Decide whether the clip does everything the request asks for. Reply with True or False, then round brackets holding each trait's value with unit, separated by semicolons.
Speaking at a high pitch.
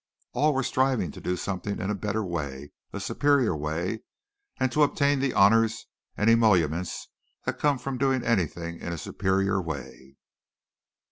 False (100 Hz)